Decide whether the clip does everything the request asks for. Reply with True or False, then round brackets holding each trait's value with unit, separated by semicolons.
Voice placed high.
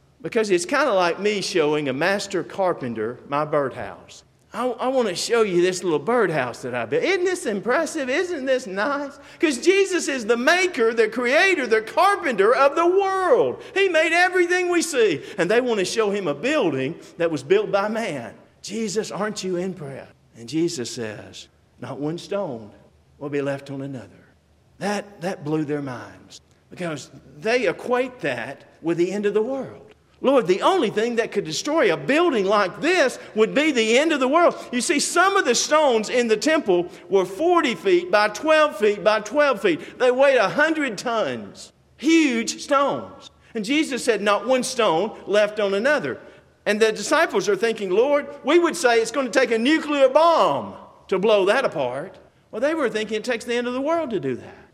True (230 Hz)